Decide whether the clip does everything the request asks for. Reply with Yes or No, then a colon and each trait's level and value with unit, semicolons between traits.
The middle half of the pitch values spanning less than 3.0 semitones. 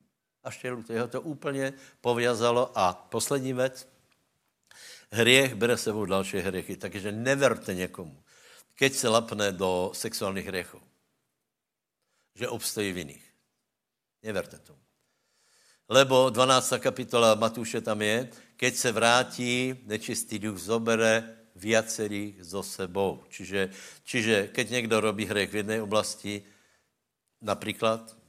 No: average, 3.5 semitones